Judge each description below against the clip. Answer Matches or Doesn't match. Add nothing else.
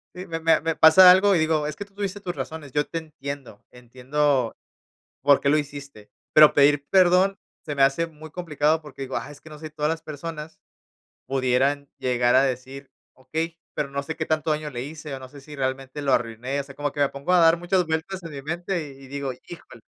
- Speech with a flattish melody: Doesn't match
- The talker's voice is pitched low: Doesn't match